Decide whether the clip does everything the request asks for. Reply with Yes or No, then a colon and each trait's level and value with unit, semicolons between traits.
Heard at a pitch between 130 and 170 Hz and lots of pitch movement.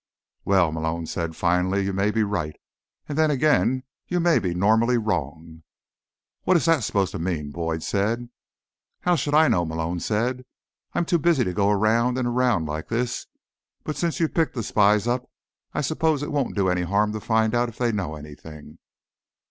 No: low, 105 Hz; wide, 6.5 semitones